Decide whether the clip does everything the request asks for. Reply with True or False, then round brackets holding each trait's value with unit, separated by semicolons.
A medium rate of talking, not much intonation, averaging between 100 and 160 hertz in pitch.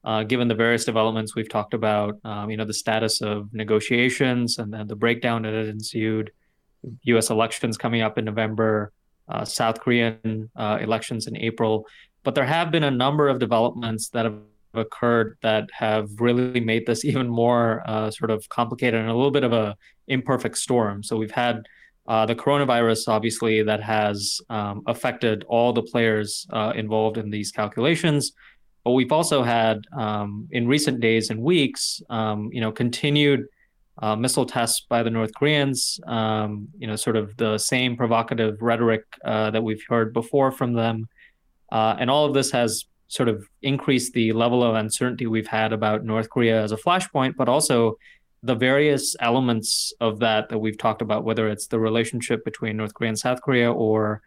True (180 wpm; 1.9 semitones; 115 Hz)